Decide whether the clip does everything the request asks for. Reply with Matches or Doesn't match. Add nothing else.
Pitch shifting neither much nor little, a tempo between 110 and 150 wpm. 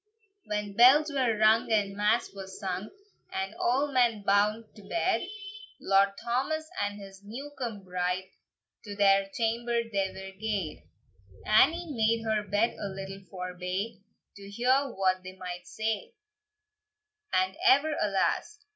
Matches